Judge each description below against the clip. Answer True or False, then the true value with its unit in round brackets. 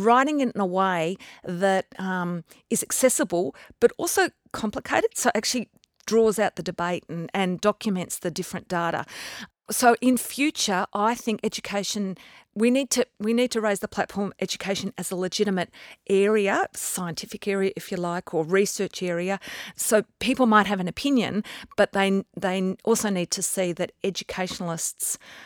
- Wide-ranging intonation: False (3.5 semitones)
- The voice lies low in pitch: False (200 Hz)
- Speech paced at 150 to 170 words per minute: True (160 wpm)